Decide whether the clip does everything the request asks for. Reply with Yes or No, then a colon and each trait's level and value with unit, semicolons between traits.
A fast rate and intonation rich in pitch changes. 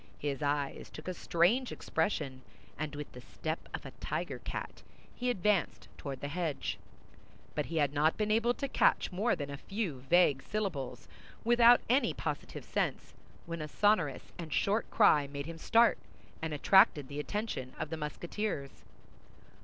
No: average, 160 wpm; wide, 6.6 semitones